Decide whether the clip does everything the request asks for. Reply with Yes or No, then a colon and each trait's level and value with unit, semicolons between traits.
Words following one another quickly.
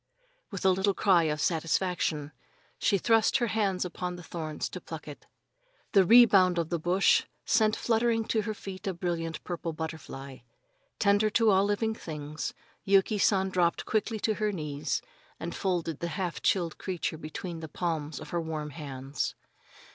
No: average, 165 wpm